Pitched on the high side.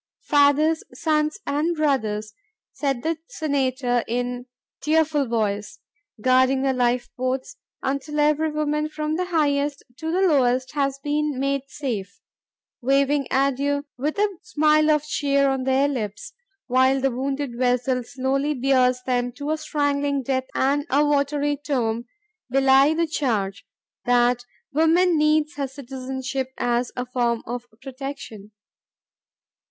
Yes: very high, 275 Hz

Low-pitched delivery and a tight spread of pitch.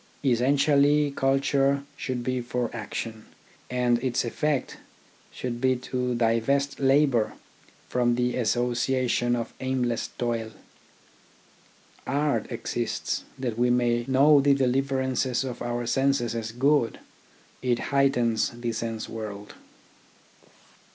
Yes: low, 125 Hz; narrow, 2.3 semitones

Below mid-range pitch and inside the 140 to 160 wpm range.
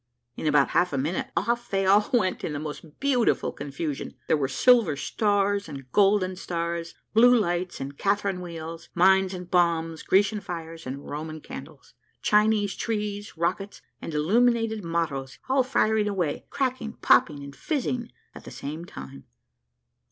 No: medium, 180 Hz; average, 150 wpm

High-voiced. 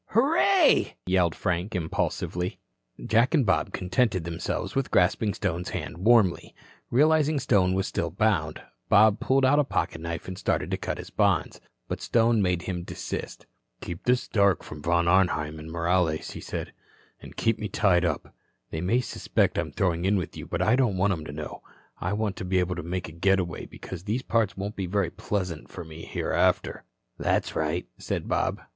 No: very low, 95 Hz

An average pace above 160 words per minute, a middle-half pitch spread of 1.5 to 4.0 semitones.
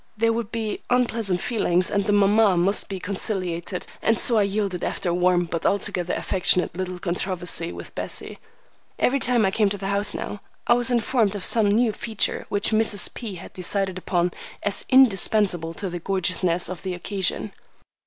Yes: average, 180 wpm; average, 3.1 semitones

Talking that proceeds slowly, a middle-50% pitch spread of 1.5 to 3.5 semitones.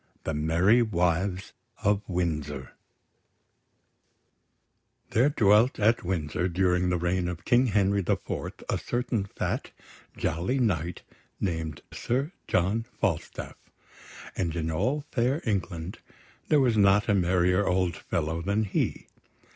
No: slow, 125 wpm; average, 4.1 semitones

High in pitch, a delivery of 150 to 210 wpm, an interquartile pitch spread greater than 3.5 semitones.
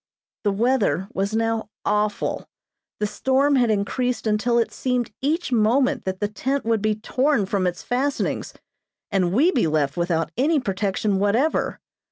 Yes: high, 220 Hz; average, 155 wpm; average, 4.5 semitones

